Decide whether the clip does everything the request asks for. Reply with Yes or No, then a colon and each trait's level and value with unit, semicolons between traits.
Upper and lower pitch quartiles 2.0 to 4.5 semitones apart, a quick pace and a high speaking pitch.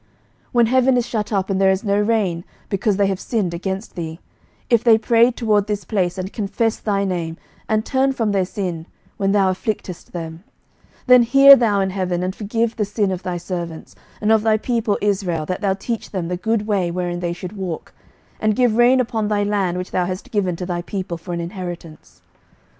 Yes: average, 3.5 semitones; fast, 215 wpm; high, 200 Hz